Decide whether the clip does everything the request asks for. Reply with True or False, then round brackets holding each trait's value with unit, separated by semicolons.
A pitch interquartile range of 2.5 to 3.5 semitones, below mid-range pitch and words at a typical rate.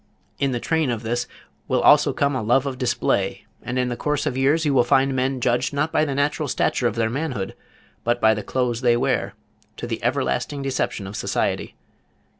False (2.8 semitones; 125 Hz; 210 wpm)